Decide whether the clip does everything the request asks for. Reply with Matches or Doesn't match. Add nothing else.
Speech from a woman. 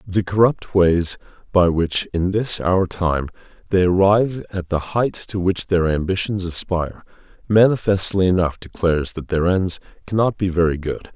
Doesn't match